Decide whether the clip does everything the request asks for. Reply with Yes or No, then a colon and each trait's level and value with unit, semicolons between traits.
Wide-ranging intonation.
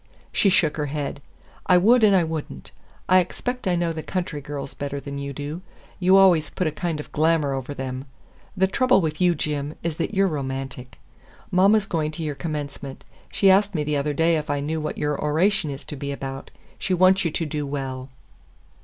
No: average, 4.2 semitones